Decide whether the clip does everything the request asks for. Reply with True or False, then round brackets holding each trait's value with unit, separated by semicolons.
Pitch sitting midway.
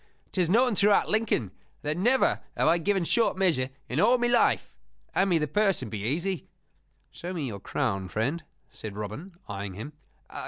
True (170 Hz)